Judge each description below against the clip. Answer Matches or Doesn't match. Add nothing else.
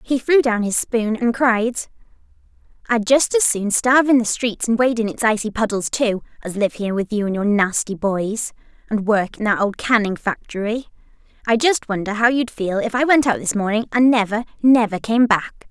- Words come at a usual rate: Doesn't match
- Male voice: Doesn't match